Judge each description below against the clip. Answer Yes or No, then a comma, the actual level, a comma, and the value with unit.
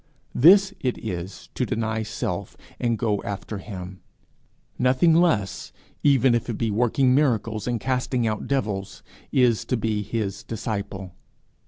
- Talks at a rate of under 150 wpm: Yes, average, 140 wpm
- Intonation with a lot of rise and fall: No, average, 3.7 semitones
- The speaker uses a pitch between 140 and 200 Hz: No, low, 115 Hz